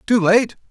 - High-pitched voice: Yes, high, 215 Hz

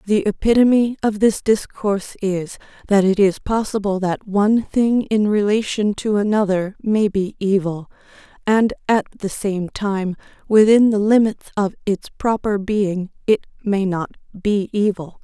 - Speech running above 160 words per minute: No, average, 145 wpm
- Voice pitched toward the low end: No, high, 205 Hz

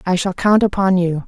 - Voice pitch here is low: No, medium, 185 Hz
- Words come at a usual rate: No, fast, 235 wpm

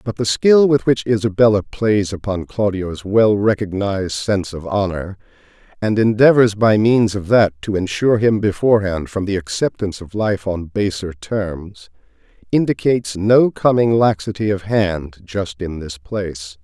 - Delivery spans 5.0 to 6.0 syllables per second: No, 4.6 syllables/s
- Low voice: Yes, low, 100 Hz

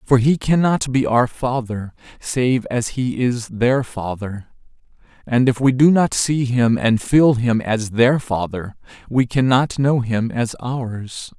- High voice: No, low, 125 Hz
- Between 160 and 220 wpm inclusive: Yes, average, 165 wpm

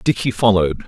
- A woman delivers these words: No, male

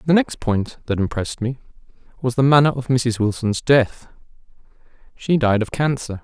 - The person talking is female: No, male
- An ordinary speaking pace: Yes, average, 165 wpm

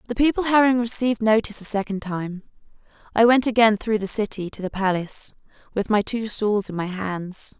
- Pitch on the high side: Yes, high, 210 Hz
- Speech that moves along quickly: No, average, 190 wpm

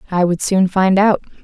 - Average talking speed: No, fast, 210 wpm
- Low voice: No, high, 190 Hz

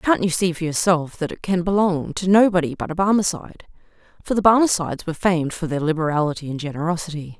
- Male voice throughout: No, female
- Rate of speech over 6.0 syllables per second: Yes, 6.5 syllables/s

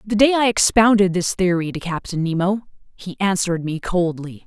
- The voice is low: No, high, 190 Hz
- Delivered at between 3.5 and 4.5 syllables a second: No, 5.3 syllables/s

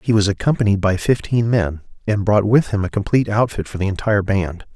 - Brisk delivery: Yes, fast, 215 wpm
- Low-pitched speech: Yes, low, 105 Hz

